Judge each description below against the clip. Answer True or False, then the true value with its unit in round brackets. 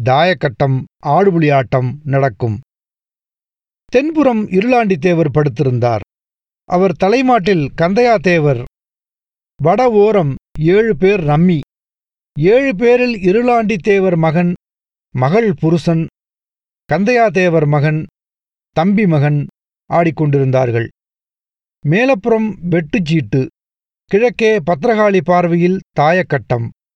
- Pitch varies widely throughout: True (6.4 semitones)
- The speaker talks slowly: True (70 wpm)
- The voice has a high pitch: False (175 Hz)